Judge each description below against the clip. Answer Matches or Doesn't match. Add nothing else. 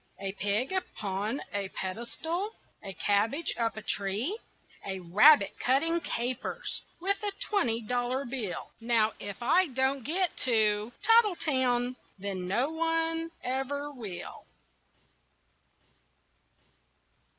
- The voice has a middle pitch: Doesn't match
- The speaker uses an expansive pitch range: Matches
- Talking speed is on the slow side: Matches